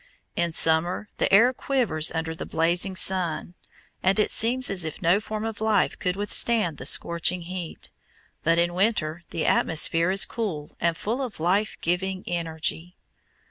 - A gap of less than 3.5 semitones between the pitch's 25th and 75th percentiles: No, average, 4.1 semitones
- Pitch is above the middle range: No, medium, 180 Hz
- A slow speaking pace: No, average, 160 wpm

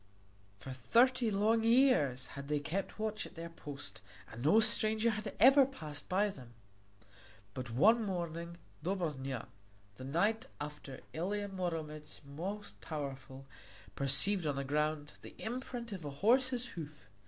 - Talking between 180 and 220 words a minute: No, average, 140 wpm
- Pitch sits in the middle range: Yes, medium, 170 Hz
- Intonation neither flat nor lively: No, wide, 7.3 semitones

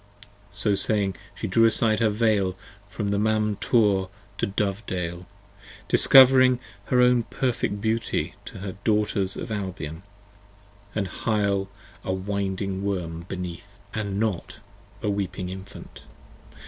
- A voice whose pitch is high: No, low, 100 Hz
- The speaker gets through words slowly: Yes, slow, 120 wpm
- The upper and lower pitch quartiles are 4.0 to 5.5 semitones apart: No, narrow, 2.5 semitones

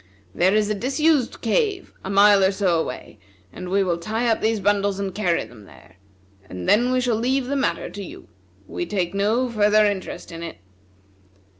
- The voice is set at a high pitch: Yes, high, 205 Hz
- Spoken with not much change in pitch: No, average, 4.2 semitones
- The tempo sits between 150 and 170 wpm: No, average, 190 wpm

